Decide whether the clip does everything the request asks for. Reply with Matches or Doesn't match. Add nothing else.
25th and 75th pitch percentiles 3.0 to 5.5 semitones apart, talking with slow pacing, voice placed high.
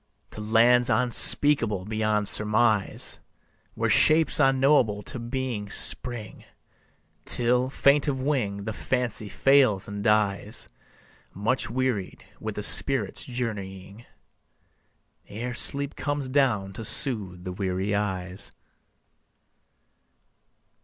Doesn't match